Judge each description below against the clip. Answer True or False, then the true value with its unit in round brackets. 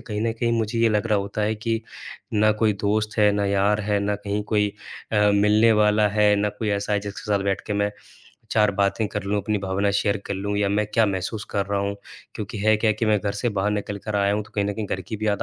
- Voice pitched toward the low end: True (105 Hz)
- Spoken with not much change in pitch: True (1.1 semitones)